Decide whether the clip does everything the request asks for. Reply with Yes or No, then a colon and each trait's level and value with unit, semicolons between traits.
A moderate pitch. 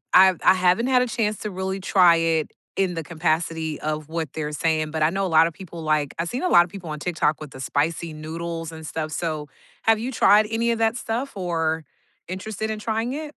Yes: medium, 170 Hz